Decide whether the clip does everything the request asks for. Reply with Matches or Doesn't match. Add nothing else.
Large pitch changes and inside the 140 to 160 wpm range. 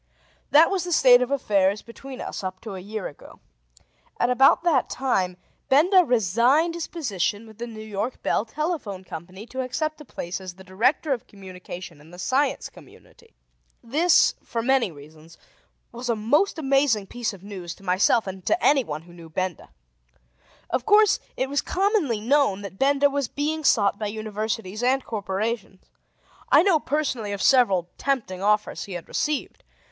Doesn't match